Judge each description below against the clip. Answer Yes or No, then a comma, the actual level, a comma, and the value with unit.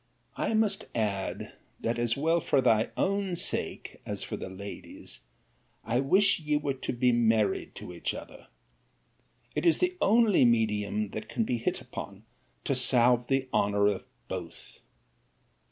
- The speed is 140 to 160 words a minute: Yes, average, 155 wpm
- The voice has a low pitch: Yes, low, 120 Hz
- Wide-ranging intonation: Yes, wide, 6.9 semitones